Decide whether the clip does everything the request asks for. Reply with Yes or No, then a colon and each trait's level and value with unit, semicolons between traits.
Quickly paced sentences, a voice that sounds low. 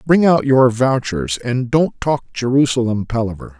No: average, 150 wpm; low, 125 Hz